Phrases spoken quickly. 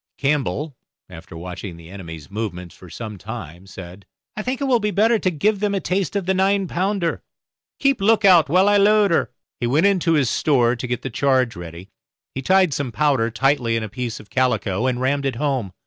Yes: fast, 215 wpm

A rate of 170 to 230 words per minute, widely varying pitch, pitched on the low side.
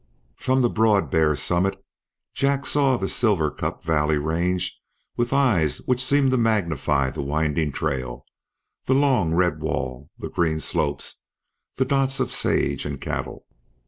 No: average, 145 wpm; wide, 8.8 semitones; very low, 90 Hz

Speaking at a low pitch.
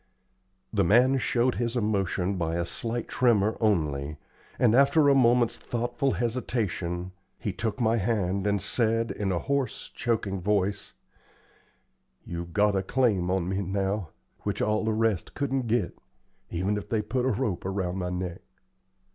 Yes: low, 105 Hz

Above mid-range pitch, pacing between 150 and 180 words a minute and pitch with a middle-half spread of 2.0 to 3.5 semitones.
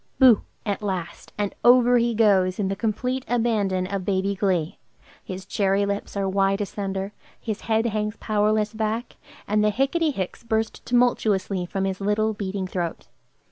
Yes: high, 205 Hz; average, 160 wpm; narrow, 2.5 semitones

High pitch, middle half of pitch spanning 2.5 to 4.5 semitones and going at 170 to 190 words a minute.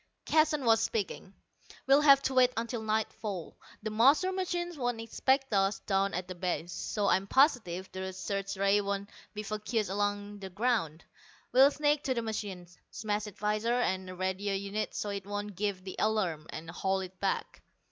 Yes: high, 205 Hz; average, 3.5 semitones; average, 175 wpm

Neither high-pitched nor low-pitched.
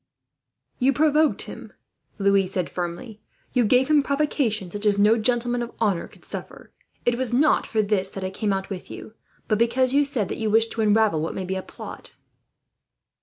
No: high, 220 Hz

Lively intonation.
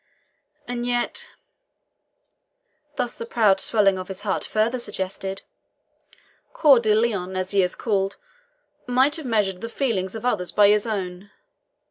No: average, 3.7 semitones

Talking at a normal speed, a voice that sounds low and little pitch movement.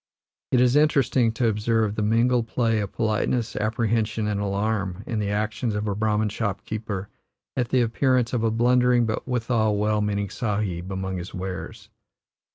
Yes: average, 165 wpm; low, 110 Hz; narrow, 2.3 semitones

